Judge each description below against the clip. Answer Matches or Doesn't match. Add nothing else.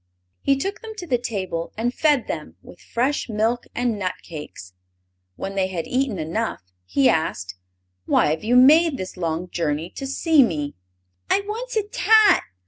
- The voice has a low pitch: Doesn't match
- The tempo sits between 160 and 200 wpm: Matches